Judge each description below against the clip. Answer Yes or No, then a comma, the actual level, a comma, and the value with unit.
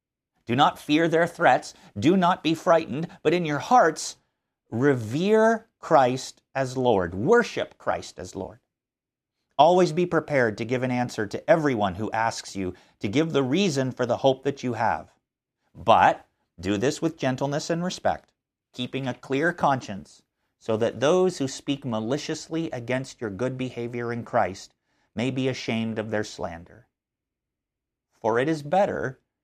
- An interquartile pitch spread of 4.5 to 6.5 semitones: Yes, wide, 5.4 semitones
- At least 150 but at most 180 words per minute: Yes, average, 155 wpm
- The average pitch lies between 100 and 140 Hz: Yes, low, 135 Hz